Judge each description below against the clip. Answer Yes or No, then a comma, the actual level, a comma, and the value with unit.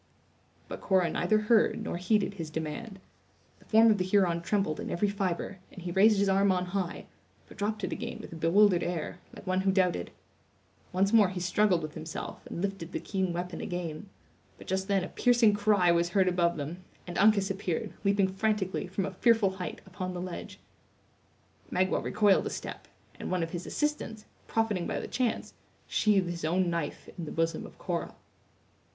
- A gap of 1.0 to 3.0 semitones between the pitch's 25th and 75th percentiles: Yes, average, 2.7 semitones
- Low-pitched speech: No, high, 190 Hz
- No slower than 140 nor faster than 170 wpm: No, average, 190 wpm